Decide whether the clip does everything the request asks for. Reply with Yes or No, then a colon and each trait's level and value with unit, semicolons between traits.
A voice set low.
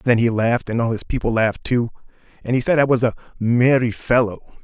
Yes: low, 120 Hz